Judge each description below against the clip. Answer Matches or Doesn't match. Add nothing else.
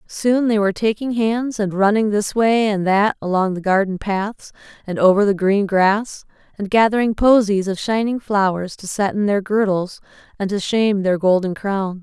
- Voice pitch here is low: Doesn't match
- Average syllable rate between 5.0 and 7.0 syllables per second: Doesn't match